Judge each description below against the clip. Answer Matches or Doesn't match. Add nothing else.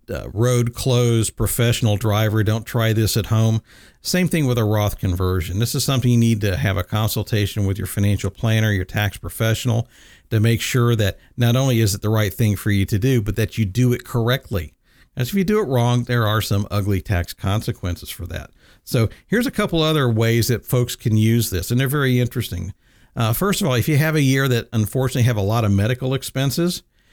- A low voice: Matches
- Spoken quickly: Matches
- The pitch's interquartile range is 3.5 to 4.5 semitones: Doesn't match